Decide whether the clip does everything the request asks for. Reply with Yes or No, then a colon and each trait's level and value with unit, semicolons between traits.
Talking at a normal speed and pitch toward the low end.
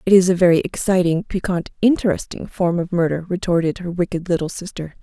No: average, 180 wpm; medium, 175 Hz